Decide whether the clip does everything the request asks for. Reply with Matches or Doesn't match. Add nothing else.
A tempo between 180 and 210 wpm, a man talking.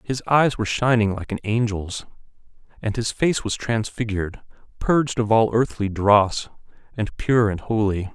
Doesn't match